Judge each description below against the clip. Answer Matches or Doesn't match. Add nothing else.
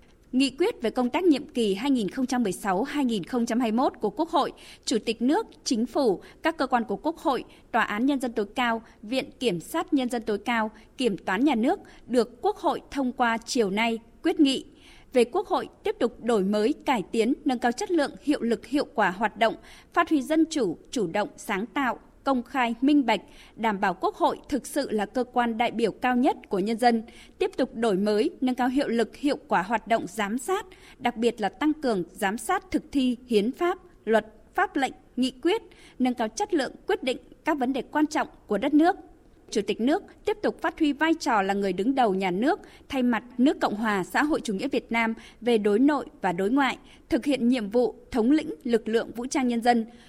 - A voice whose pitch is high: Matches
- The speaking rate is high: Doesn't match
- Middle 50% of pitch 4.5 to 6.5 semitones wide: Matches